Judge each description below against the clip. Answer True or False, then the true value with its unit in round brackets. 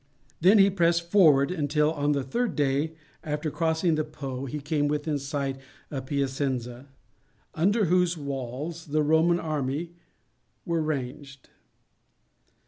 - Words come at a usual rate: False (130 wpm)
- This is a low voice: False (150 Hz)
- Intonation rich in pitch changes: False (3.2 semitones)